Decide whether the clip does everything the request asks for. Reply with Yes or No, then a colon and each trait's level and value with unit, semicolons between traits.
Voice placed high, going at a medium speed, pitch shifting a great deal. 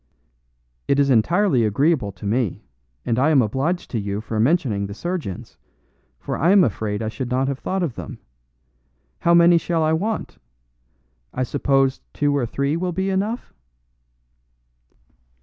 No: medium, 140 Hz; average, 155 wpm; wide, 7.0 semitones